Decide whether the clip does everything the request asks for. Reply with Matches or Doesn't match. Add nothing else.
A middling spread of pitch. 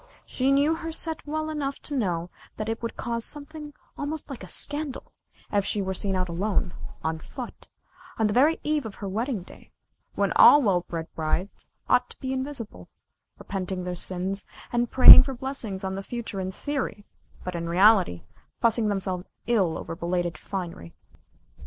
Doesn't match